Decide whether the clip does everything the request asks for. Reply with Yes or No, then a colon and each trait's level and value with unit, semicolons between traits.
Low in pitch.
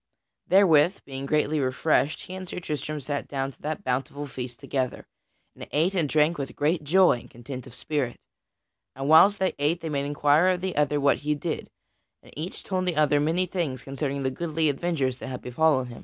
No: medium, 150 Hz